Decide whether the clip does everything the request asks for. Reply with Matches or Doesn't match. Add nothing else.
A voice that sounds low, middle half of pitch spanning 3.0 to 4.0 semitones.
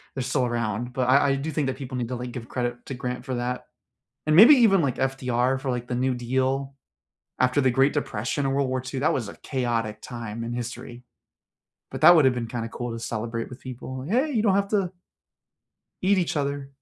Doesn't match